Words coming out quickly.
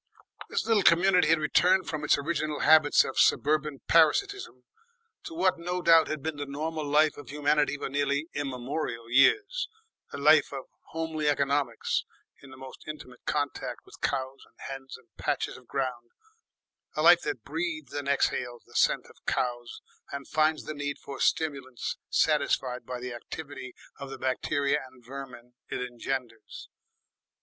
No: average, 160 wpm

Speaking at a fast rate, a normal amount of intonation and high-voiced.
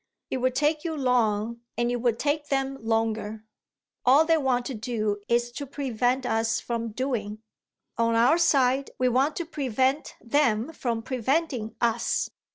No: average, 160 wpm; average, 3.3 semitones; high, 245 Hz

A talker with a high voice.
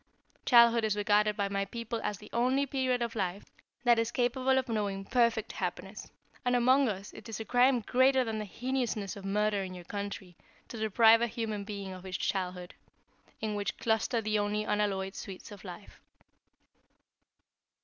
Yes: high, 215 Hz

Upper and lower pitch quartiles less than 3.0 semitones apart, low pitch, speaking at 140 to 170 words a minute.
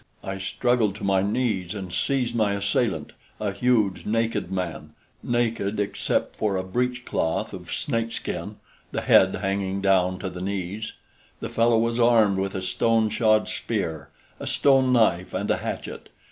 No: average, 3.5 semitones; low, 100 Hz; average, 155 wpm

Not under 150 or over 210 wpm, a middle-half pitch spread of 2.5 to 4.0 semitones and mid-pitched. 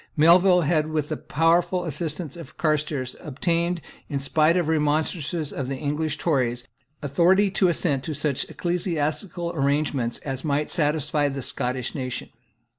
No: average, 140 wpm; average, 3.3 semitones; medium, 155 Hz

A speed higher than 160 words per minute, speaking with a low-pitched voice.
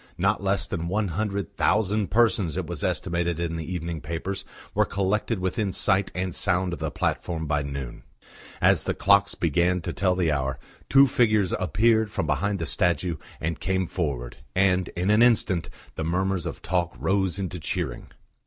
Yes: average, 175 wpm; very low, 90 Hz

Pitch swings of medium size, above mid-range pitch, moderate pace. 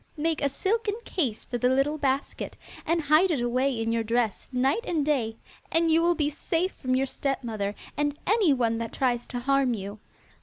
Yes: average, 4.7 semitones; very high, 275 Hz; average, 190 wpm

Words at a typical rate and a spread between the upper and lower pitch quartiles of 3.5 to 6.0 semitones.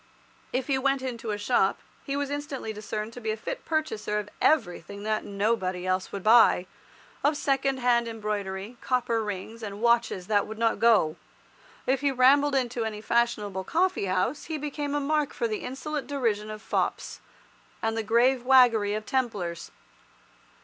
Yes: average, 170 wpm; average, 4.3 semitones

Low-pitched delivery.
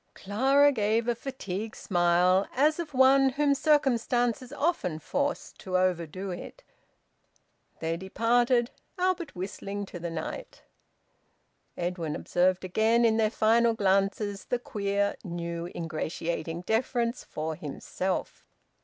No: high, 210 Hz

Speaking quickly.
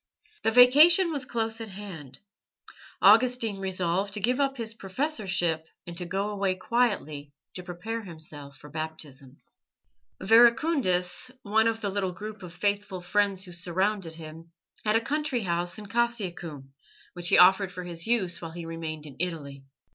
No: average, 155 wpm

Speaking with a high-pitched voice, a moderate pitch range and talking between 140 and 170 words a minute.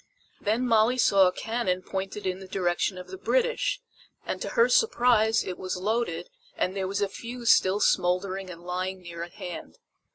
No: high, 195 Hz; average, 4.1 semitones; average, 185 wpm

